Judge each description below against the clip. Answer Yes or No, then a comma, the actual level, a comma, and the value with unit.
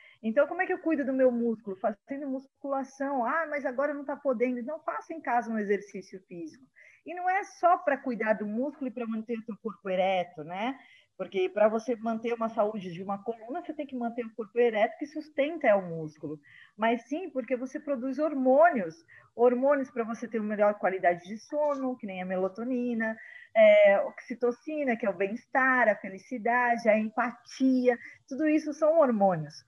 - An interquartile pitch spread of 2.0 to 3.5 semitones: No, average, 5.2 semitones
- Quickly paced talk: Yes, fast, 190 wpm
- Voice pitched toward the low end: No, high, 245 Hz